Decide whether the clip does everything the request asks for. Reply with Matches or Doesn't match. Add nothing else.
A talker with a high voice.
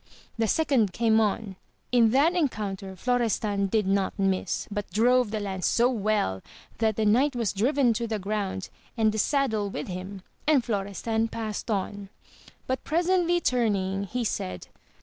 Matches